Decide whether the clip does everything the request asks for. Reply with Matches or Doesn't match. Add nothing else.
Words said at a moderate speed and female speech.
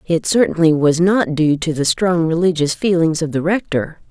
Matches